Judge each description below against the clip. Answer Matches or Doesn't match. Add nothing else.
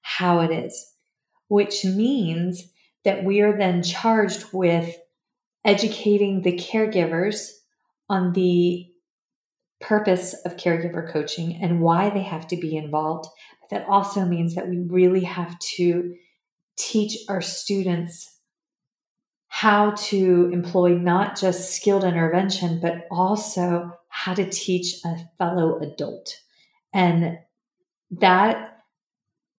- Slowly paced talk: Matches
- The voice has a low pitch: Doesn't match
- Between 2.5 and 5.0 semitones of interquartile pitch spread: Matches